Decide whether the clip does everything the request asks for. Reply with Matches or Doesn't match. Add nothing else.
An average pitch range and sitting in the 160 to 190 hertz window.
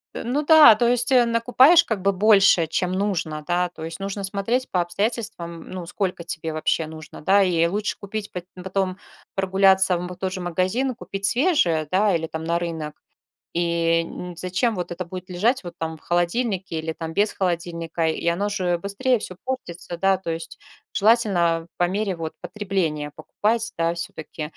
Matches